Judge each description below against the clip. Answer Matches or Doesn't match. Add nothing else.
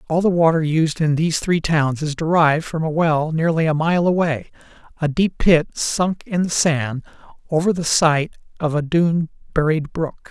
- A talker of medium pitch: Matches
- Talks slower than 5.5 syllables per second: Matches